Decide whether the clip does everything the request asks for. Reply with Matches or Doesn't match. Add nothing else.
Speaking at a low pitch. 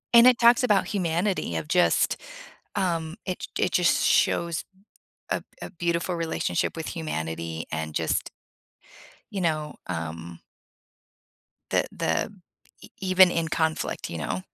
Doesn't match